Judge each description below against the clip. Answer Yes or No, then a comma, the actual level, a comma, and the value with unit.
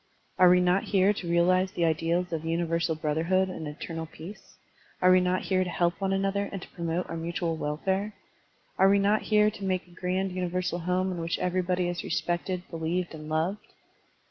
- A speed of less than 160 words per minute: No, average, 195 wpm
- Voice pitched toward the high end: No, medium, 180 Hz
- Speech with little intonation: Yes, narrow, 2.1 semitones